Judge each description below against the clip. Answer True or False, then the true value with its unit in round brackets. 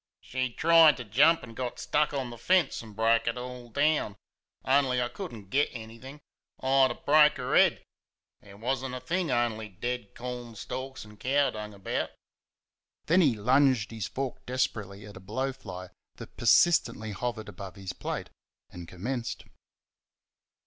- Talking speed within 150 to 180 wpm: True (160 wpm)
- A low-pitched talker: True (125 Hz)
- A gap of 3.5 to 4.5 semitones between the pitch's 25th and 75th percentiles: True (4.0 semitones)